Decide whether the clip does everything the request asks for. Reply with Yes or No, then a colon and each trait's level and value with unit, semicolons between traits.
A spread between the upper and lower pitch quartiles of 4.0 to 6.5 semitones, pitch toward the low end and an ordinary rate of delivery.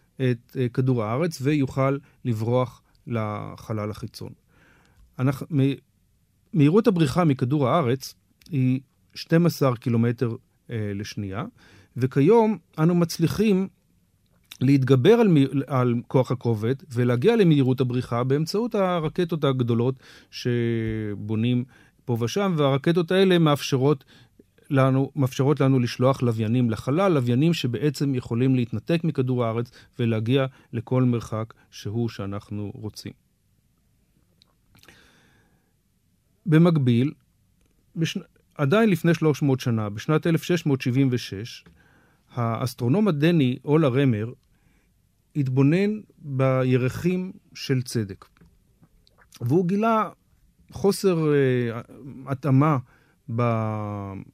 No: average, 4.5 semitones; low, 130 Hz; slow, 85 wpm